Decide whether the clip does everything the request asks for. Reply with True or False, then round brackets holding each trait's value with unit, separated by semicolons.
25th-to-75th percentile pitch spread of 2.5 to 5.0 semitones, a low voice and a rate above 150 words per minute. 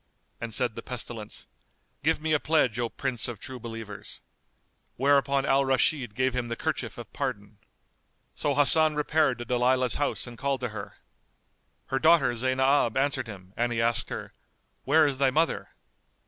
True (3.1 semitones; 130 Hz; 165 wpm)